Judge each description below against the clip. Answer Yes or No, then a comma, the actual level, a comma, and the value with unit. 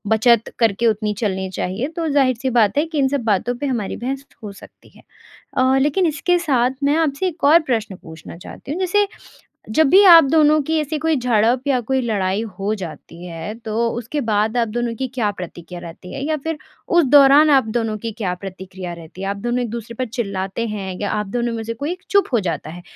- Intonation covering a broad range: Yes, wide, 5.8 semitones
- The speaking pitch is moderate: No, high, 235 Hz